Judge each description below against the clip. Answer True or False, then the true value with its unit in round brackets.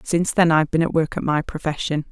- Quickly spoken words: True (255 wpm)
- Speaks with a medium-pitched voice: True (160 Hz)